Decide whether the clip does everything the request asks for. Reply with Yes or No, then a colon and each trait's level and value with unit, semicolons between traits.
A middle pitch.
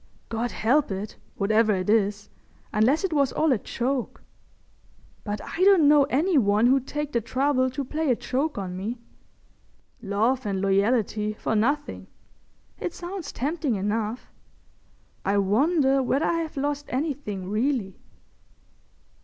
No: very high, 250 Hz